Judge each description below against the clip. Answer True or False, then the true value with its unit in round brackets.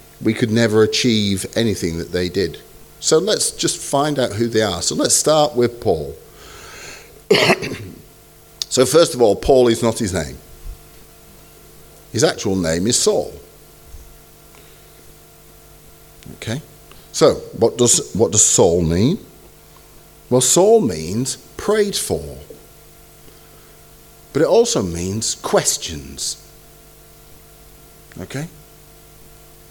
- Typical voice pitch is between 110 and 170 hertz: False (100 Hz)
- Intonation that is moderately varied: False (8.2 semitones)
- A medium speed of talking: False (110 wpm)